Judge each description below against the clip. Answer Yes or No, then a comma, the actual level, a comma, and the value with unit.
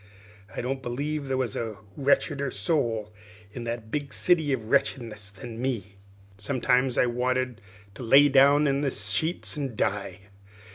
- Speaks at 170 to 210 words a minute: No, average, 150 wpm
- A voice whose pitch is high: No, low, 125 Hz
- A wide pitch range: No, average, 4.0 semitones